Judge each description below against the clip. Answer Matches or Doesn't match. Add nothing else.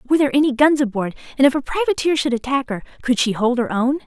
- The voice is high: Matches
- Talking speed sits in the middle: Doesn't match